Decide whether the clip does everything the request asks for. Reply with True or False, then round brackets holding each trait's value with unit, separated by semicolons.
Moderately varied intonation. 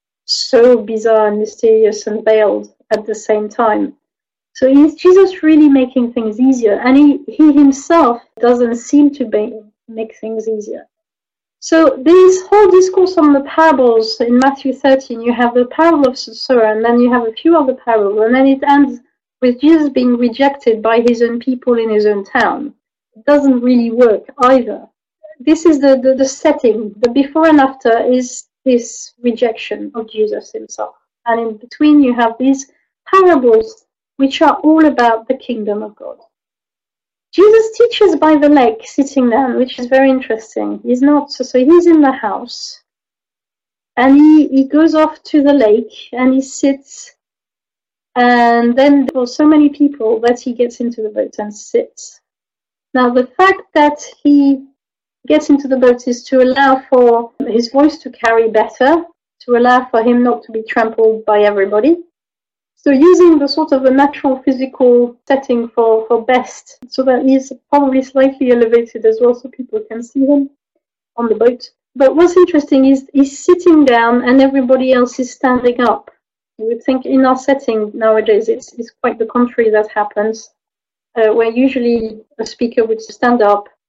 True (3.7 semitones)